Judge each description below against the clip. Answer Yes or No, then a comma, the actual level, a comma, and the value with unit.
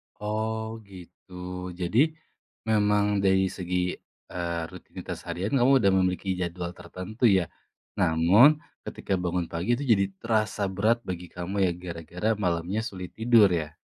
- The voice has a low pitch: Yes, very low, 95 Hz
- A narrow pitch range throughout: No, average, 3.6 semitones